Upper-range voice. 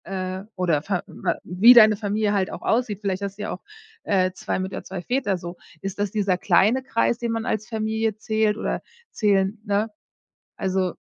Yes: high, 205 Hz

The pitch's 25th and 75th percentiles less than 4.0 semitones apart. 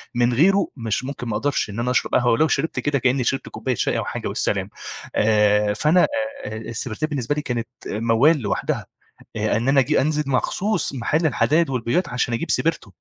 No: average, 4.5 semitones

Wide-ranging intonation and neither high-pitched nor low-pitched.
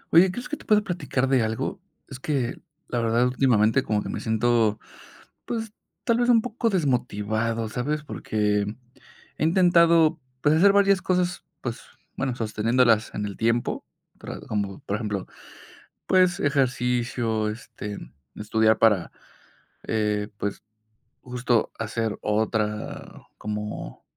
No: wide, 6.4 semitones; low, 120 Hz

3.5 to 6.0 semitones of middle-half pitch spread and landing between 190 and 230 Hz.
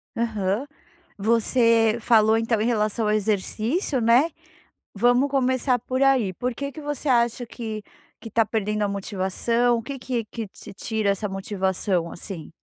No: average, 2.9 semitones; high, 225 Hz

